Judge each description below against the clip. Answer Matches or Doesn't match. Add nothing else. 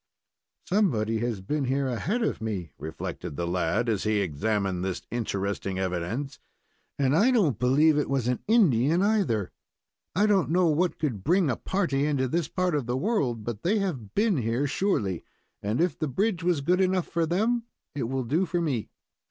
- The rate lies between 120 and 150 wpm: Doesn't match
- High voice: Doesn't match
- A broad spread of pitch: Matches